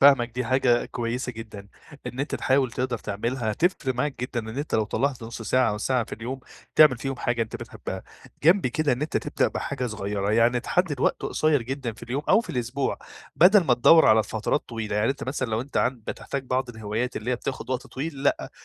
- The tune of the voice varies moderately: Yes, average, 3.1 semitones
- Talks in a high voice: No, low, 125 Hz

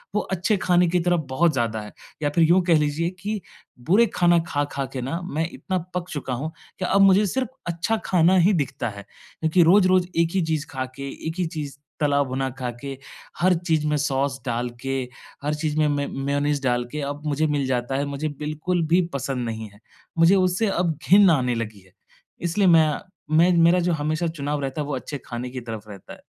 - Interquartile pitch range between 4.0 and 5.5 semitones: Yes, average, 4.5 semitones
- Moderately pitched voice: Yes, medium, 150 Hz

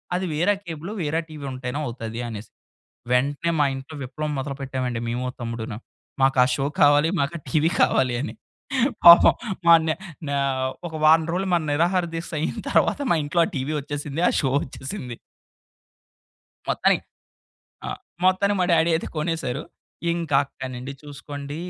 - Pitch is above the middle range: No, medium, 145 Hz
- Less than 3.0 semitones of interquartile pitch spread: No, average, 3.9 semitones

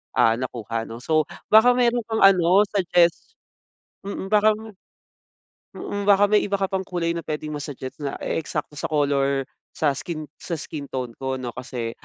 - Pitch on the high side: No, medium, 155 Hz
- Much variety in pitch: Yes, wide, 6.6 semitones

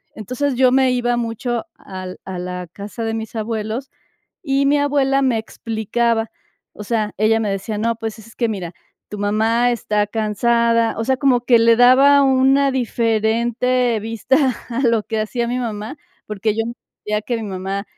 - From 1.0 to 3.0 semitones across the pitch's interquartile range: Yes, narrow, 2.6 semitones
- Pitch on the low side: No, high, 230 Hz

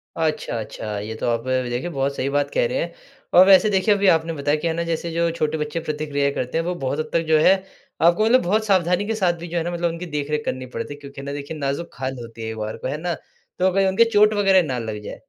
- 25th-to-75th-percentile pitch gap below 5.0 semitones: Yes, average, 4.5 semitones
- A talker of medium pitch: Yes, medium, 160 Hz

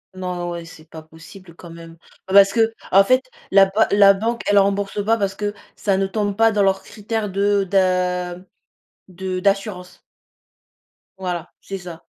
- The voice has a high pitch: Yes, high, 195 Hz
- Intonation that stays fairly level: Yes, narrow, 2.1 semitones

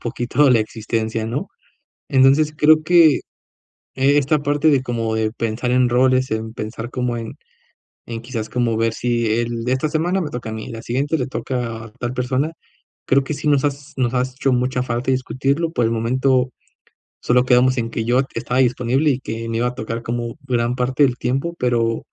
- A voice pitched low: Yes, low, 125 Hz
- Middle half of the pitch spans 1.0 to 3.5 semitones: Yes, narrow, 2.6 semitones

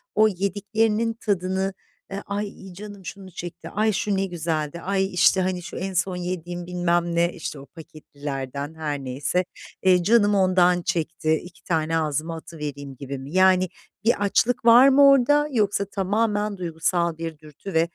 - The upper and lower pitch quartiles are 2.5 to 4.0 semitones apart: Yes, average, 3.7 semitones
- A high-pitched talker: No, medium, 180 Hz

